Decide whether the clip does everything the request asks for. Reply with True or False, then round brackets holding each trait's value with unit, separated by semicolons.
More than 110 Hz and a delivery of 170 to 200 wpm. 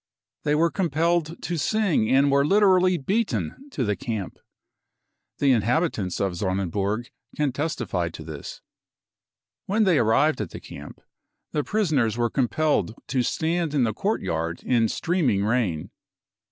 False (135 Hz; 140 wpm)